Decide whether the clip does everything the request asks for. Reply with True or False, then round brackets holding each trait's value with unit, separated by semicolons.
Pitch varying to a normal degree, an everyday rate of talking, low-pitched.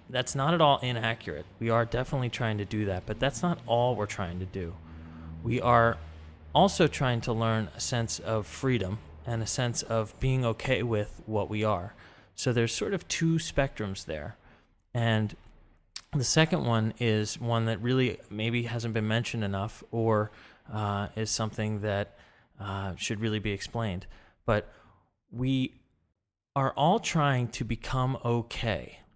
True (3.4 semitones; 160 wpm; 115 Hz)